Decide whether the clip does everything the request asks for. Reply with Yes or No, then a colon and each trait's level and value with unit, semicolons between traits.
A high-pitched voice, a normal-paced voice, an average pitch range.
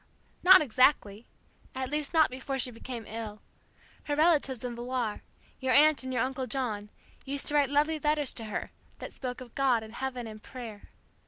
Yes: very high, 260 Hz; average, 185 wpm; average, 3.7 semitones